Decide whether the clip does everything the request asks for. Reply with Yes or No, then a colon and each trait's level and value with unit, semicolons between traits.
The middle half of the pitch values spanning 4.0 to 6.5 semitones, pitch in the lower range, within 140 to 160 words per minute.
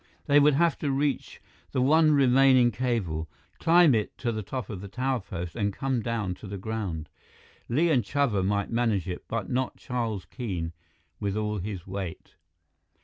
No: average, 5.2 semitones; low, 115 Hz; average, 175 wpm